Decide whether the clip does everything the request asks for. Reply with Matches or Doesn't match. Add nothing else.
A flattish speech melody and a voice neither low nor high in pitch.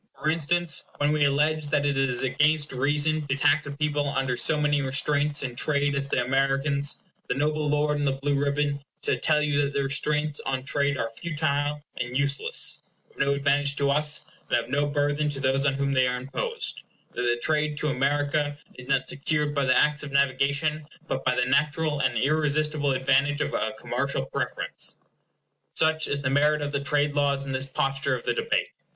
Matches